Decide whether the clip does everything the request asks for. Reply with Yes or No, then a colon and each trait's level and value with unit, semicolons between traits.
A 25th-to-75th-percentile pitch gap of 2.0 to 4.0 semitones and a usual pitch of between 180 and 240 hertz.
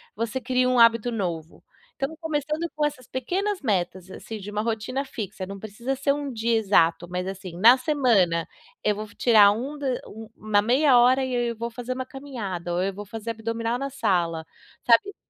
No: average, 4.7 semitones; high, 230 Hz